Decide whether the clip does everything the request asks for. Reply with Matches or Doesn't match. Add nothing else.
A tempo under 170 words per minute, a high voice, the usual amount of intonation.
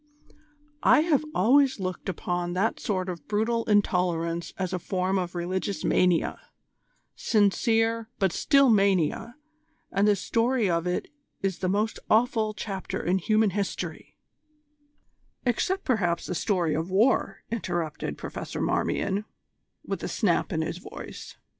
Matches